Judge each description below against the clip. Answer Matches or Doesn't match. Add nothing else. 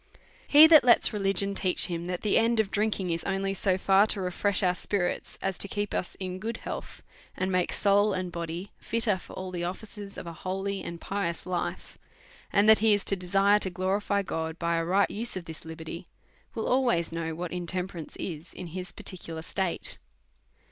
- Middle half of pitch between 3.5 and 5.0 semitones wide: Doesn't match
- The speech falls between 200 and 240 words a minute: Matches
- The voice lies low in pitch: Doesn't match